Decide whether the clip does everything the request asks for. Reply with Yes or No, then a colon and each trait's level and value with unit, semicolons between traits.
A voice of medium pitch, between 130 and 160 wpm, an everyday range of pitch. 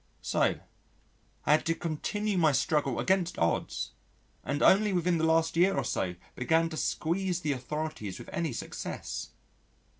Yes: medium, 160 Hz; average, 150 wpm; average, 3.2 semitones